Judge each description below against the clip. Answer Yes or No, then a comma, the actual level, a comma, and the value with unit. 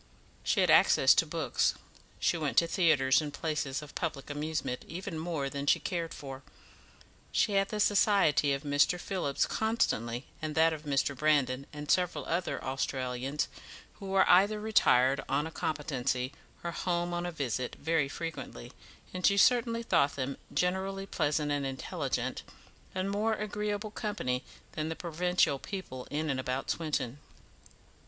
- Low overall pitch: No, medium, 155 Hz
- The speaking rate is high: No, average, 155 wpm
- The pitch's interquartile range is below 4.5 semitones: No, average, 5.0 semitones